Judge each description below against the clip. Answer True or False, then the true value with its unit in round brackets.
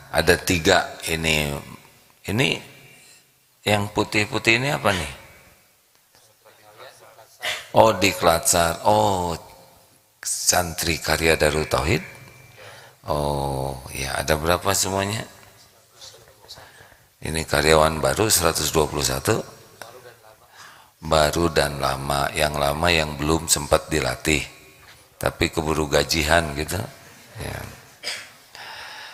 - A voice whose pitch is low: True (80 Hz)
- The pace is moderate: False (80 wpm)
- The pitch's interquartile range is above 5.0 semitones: False (3.3 semitones)